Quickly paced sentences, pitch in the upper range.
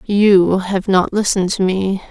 No: average, 170 wpm; high, 195 Hz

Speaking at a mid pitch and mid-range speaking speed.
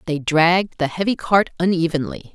Yes: medium, 170 Hz; average, 155 wpm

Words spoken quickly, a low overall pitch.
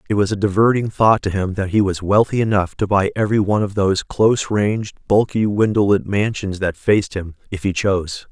Yes: fast, 215 wpm; low, 100 Hz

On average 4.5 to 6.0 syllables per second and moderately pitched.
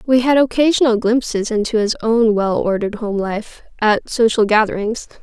No: 5.0 syllables/s; high, 225 Hz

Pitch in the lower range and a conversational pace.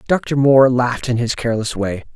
Yes: low, 120 Hz; average, 195 wpm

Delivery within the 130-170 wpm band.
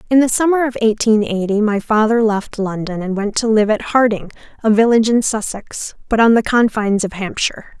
No: average, 200 wpm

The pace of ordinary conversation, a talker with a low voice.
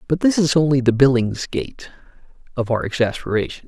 Yes: average, 145 wpm; low, 130 Hz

